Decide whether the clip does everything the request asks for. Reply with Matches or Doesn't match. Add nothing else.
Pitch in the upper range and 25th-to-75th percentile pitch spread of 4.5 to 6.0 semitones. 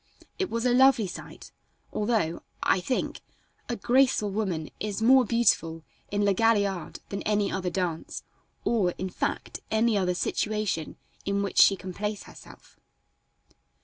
Doesn't match